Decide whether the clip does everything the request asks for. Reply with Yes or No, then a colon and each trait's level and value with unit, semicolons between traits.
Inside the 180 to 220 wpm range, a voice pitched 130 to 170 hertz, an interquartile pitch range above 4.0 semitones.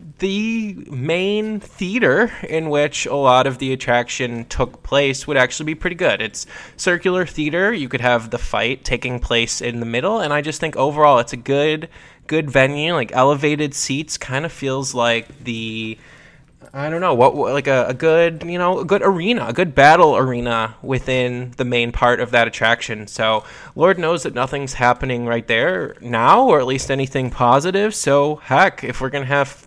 Yes: average, 185 wpm; medium, 140 Hz; average, 4.5 semitones